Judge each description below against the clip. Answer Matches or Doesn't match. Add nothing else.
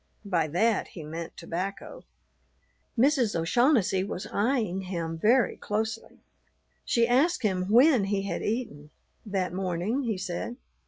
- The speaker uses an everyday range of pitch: Matches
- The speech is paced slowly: Matches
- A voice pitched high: Matches